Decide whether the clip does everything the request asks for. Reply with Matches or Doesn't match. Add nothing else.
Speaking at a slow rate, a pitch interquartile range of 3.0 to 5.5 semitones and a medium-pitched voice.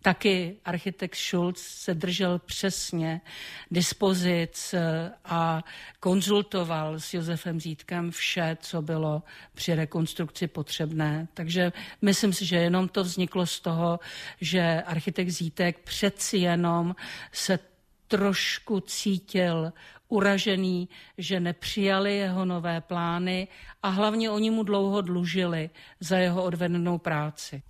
Doesn't match